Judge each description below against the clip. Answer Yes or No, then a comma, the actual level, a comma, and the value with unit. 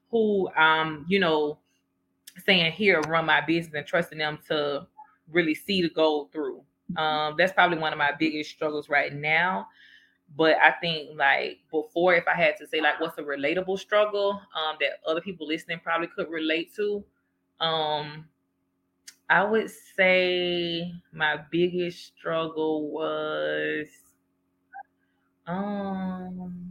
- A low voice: No, medium, 160 Hz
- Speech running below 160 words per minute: Yes, average, 140 wpm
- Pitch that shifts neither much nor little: Yes, average, 3.2 semitones